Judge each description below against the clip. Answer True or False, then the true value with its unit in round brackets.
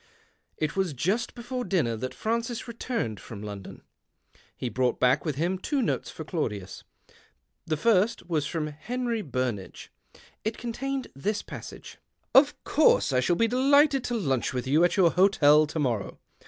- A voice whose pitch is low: False (175 Hz)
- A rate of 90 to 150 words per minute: False (165 wpm)